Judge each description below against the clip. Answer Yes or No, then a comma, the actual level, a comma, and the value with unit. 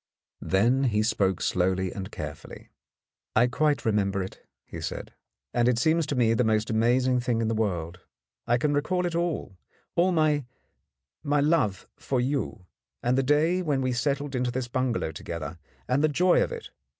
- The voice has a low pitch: Yes, low, 125 Hz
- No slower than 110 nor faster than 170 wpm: No, average, 180 wpm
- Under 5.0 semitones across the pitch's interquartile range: No, wide, 5.4 semitones